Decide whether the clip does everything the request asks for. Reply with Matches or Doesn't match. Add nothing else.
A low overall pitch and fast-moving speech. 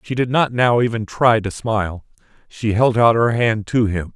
Matches